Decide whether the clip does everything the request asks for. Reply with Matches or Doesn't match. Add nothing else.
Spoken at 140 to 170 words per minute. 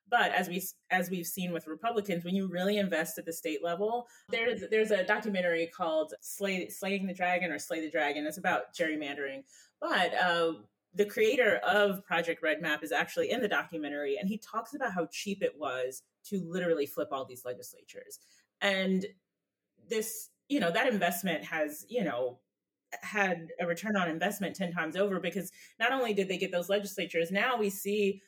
Doesn't match